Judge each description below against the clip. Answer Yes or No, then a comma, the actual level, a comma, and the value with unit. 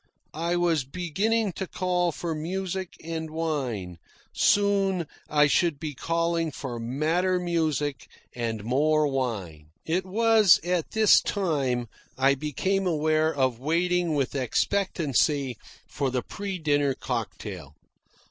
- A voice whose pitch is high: No, medium, 155 Hz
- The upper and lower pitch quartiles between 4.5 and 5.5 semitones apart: Yes, average, 5.0 semitones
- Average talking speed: No, slow, 120 wpm